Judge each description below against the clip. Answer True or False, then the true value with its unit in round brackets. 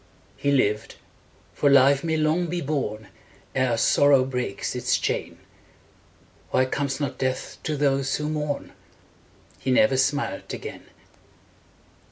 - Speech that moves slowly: True (125 wpm)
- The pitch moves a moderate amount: False (2.3 semitones)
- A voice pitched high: False (140 Hz)